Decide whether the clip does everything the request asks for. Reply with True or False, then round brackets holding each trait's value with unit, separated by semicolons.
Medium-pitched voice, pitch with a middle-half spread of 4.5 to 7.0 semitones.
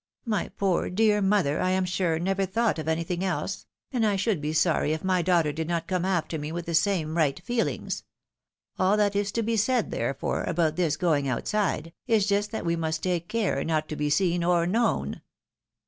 False (180 Hz; 4.0 semitones)